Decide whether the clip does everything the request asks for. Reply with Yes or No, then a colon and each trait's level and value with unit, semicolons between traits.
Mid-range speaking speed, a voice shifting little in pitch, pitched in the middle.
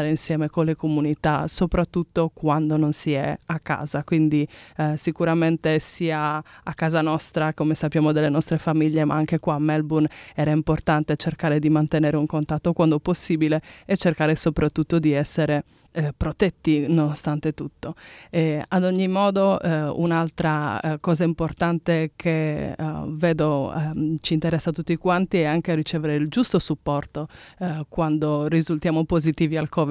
Yes: average, 155 wpm; narrow, 1.5 semitones; medium, 155 Hz